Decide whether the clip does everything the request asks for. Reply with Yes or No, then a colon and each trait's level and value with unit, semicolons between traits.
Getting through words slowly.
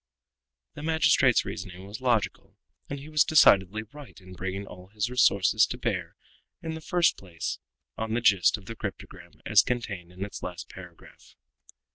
No: average, 165 wpm